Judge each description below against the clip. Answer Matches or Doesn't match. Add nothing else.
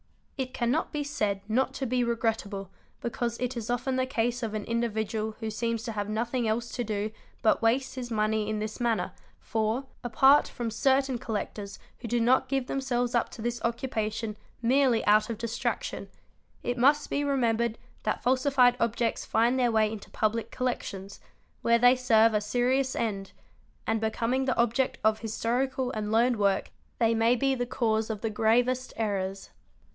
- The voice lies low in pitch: Doesn't match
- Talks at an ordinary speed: Matches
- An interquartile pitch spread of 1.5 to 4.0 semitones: Matches